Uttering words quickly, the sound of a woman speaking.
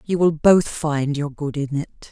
Yes: fast, 225 wpm; female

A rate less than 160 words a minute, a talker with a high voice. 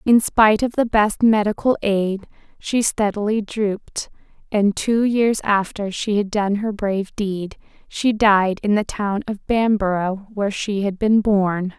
No: average, 165 wpm; high, 205 Hz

